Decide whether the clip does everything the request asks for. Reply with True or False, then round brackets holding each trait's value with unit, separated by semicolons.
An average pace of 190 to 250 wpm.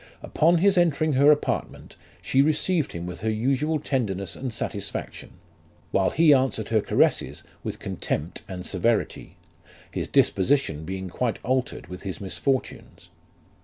False (135 wpm)